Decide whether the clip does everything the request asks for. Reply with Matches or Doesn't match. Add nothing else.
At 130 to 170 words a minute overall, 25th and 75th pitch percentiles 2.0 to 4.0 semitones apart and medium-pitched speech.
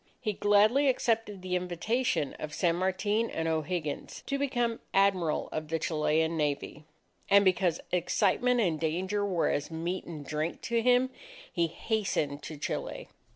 Doesn't match